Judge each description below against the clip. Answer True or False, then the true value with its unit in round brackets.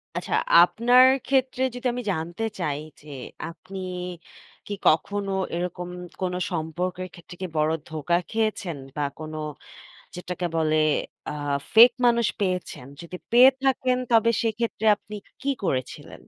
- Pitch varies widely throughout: True (5.8 semitones)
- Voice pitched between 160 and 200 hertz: True (185 Hz)